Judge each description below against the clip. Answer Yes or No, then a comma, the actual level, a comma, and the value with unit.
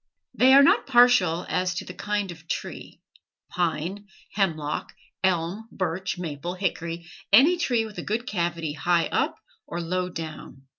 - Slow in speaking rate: No, average, 150 wpm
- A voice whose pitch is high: No, medium, 180 Hz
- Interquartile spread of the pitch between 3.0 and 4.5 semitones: Yes, average, 3.9 semitones